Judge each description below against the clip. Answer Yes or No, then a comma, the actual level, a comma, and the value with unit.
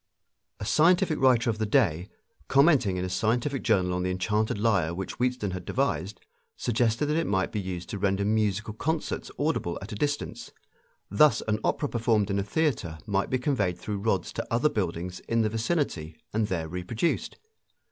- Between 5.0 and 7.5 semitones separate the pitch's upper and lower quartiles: Yes, average, 5.3 semitones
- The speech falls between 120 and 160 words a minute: No, average, 180 wpm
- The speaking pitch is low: Yes, low, 105 Hz